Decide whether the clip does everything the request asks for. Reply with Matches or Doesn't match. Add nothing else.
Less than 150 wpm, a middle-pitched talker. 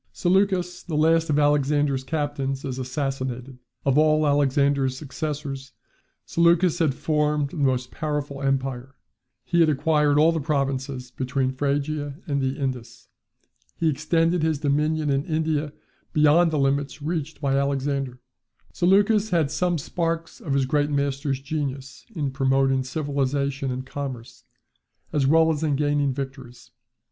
Matches